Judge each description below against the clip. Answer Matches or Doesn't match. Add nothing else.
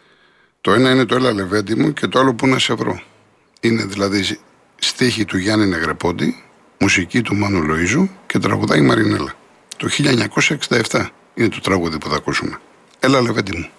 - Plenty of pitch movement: Doesn't match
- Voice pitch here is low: Matches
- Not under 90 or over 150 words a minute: Doesn't match